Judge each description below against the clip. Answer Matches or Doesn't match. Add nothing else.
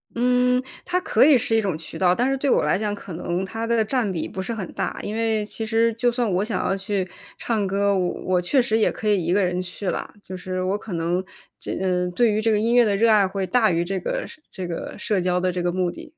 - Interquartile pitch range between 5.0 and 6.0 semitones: Doesn't match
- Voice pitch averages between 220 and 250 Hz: Doesn't match